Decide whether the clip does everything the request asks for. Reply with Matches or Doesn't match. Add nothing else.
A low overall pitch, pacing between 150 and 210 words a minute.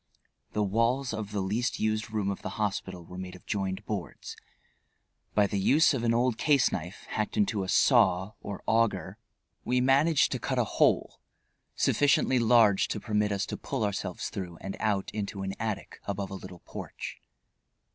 Matches